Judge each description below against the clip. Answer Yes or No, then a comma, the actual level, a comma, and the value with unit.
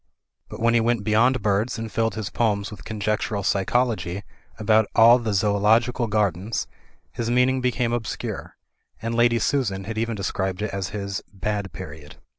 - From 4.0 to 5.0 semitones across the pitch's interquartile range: No, average, 2.7 semitones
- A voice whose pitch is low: Yes, low, 110 Hz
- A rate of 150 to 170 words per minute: Yes, average, 160 wpm